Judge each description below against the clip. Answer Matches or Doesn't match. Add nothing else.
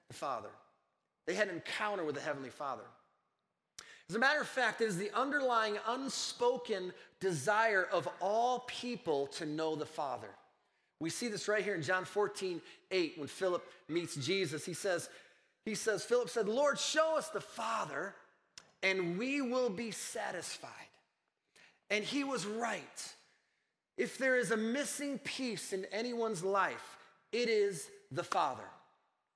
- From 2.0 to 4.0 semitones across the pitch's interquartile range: Doesn't match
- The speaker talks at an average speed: Matches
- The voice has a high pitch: Matches